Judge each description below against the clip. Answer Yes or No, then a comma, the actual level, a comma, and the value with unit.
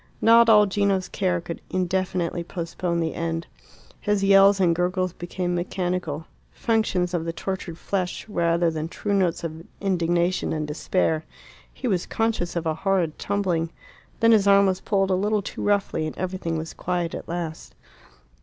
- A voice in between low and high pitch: Yes, medium, 180 Hz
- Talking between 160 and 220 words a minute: Yes, average, 165 wpm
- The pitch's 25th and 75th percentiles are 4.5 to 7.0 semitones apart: No, average, 2.7 semitones